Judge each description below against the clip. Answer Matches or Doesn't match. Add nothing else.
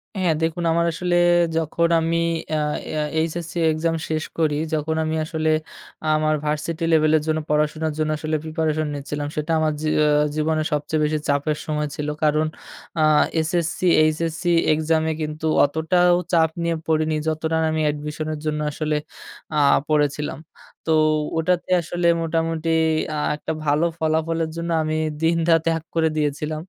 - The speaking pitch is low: Doesn't match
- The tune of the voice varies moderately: Doesn't match